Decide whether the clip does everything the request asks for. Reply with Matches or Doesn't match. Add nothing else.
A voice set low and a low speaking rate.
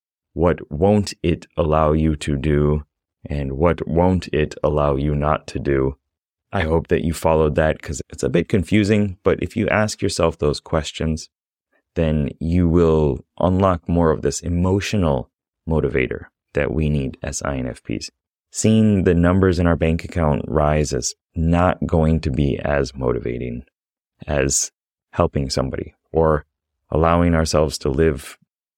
Doesn't match